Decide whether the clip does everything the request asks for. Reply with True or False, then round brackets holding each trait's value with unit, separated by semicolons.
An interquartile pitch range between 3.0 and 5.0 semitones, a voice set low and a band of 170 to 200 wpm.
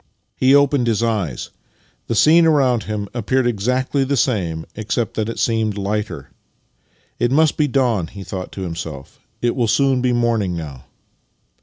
True (4.5 semitones; 115 Hz; 175 wpm)